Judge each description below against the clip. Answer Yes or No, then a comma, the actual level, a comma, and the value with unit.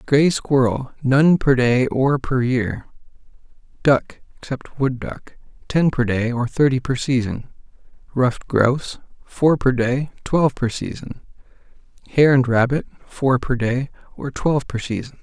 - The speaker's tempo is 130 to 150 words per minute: Yes, average, 145 wpm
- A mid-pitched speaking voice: No, low, 130 Hz